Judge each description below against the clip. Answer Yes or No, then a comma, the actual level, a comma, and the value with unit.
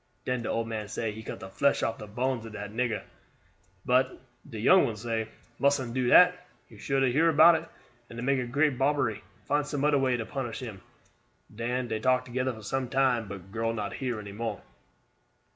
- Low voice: Yes, low, 120 Hz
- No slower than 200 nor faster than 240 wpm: Yes, fast, 205 wpm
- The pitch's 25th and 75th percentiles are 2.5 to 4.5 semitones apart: Yes, average, 3.2 semitones